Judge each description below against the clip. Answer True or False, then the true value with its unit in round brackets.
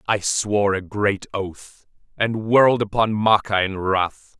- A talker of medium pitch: False (105 Hz)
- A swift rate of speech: False (150 wpm)